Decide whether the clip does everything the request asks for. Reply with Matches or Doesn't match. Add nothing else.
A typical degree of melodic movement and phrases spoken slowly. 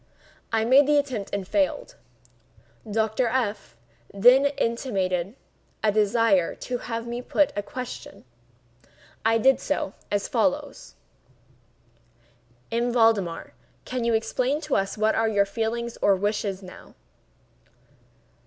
Matches